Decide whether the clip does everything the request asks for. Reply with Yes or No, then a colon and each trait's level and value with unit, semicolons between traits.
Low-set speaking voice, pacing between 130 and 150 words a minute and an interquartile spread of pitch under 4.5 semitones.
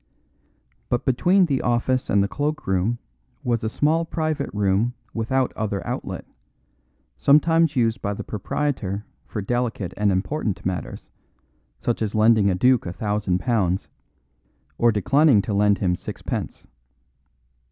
No: low, 115 Hz; slow, 135 wpm; average, 4.8 semitones